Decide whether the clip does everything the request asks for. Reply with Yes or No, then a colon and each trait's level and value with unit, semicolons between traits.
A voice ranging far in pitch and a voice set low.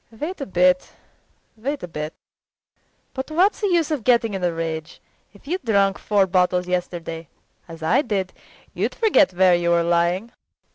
No: wide, 6.7 semitones; high, 190 Hz